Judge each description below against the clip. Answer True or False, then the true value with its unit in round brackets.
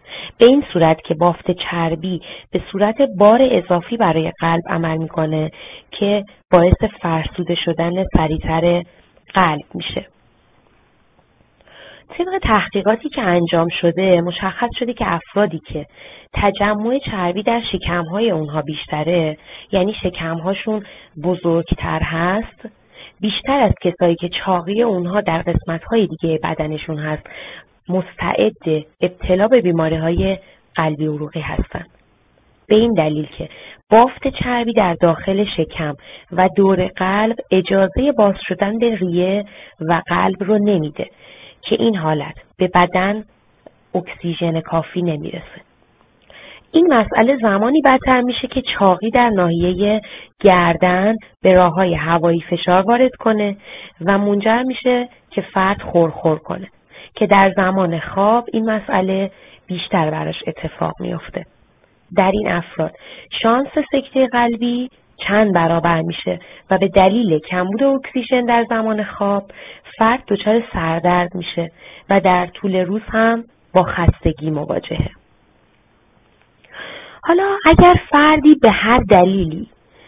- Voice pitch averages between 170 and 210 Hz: True (190 Hz)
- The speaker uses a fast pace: False (120 wpm)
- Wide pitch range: False (4.6 semitones)